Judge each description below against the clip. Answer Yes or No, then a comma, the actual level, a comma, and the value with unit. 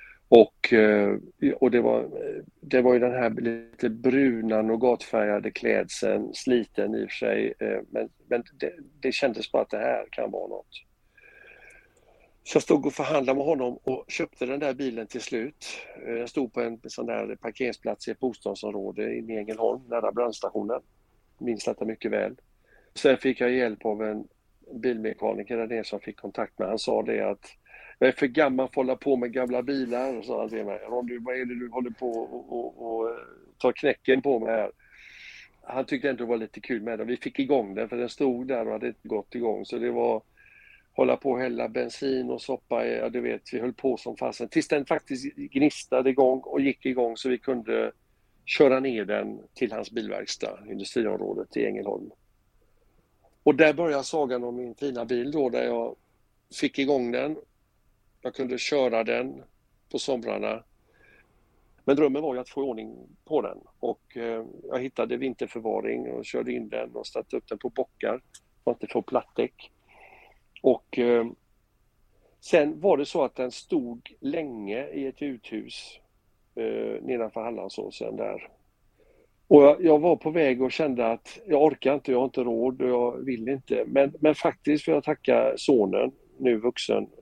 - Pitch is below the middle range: Yes, low, 130 Hz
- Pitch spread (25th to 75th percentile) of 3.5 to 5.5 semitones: Yes, average, 3.8 semitones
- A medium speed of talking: Yes, average, 180 wpm